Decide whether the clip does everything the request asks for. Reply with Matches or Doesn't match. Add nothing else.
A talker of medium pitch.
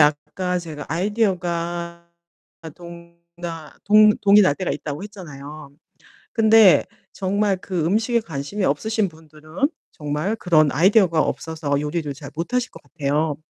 Matches